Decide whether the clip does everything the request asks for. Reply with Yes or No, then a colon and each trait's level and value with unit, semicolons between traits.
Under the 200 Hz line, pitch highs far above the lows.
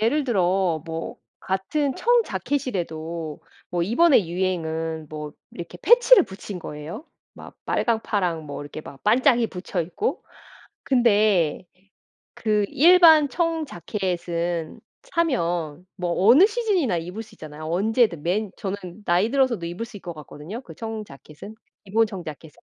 Yes: high, 190 Hz; wide, 6.3 semitones